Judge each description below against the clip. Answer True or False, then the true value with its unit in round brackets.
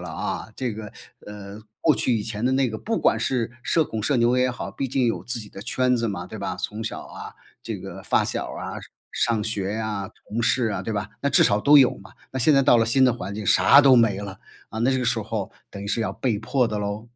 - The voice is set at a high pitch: False (115 Hz)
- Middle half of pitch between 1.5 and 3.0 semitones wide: False (3.5 semitones)